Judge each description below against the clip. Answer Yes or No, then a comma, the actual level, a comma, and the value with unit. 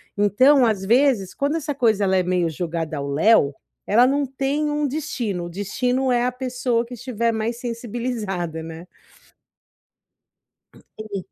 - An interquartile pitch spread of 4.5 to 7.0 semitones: Yes, wide, 5.4 semitones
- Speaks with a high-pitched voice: Yes, high, 230 Hz